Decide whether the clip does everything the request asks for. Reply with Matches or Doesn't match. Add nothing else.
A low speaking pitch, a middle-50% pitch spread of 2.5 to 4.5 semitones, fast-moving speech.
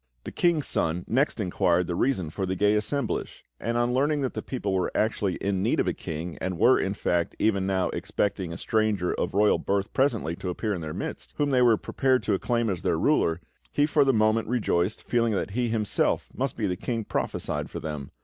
Doesn't match